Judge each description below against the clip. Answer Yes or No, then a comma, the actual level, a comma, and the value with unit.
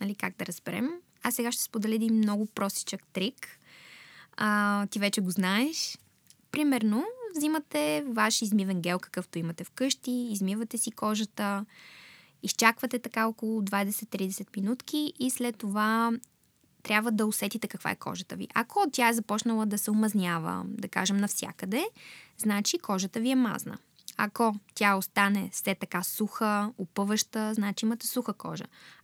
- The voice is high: Yes, high, 215 Hz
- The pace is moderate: Yes, average, 145 wpm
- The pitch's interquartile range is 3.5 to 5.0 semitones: No, average, 2.8 semitones